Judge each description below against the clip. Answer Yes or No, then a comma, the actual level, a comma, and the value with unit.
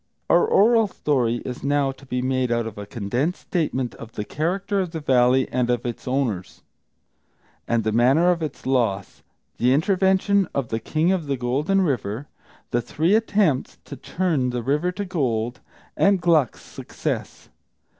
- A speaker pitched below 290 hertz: Yes, low, 135 Hz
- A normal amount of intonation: No, wide, 6.4 semitones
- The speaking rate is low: No, average, 165 wpm